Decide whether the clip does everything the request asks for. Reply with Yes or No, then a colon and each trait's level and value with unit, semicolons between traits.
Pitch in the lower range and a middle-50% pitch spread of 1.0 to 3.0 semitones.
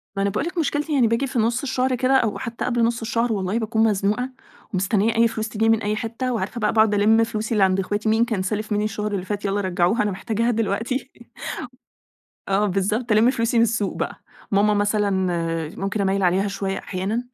No: high, 215 Hz; narrow, 2.5 semitones